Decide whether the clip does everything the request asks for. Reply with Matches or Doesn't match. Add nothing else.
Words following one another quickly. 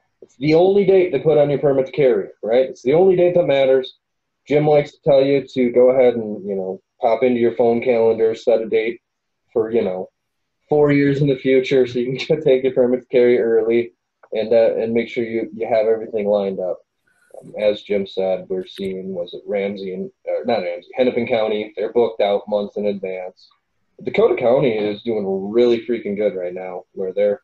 Matches